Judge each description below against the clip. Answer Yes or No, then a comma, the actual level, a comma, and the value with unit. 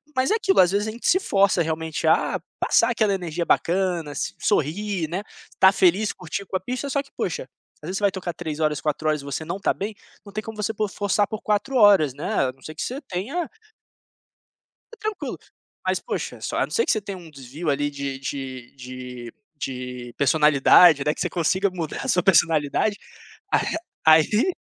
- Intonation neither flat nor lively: No, wide, 5.7 semitones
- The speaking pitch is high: No, medium, 180 Hz